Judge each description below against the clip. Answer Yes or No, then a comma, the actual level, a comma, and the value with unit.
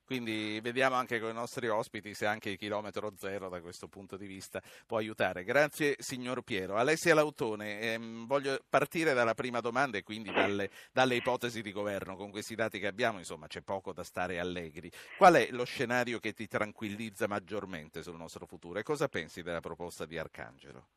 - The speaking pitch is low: Yes, low, 110 Hz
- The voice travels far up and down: No, average, 3.8 semitones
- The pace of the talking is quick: Yes, fast, 190 wpm